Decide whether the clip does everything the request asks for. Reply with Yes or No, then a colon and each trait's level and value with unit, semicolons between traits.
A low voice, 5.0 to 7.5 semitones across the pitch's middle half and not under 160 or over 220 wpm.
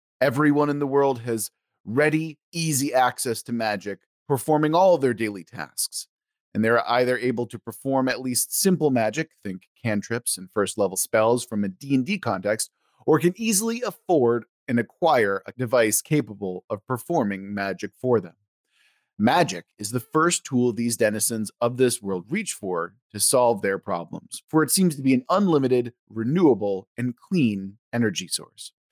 Yes: low, 120 Hz; wide, 5.5 semitones; average, 165 wpm